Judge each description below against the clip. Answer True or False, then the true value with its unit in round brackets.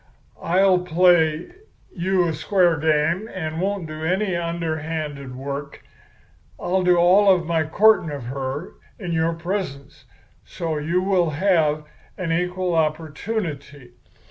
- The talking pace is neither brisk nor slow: False (125 wpm)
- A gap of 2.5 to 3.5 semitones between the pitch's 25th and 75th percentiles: True (3.1 semitones)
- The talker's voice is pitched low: False (165 Hz)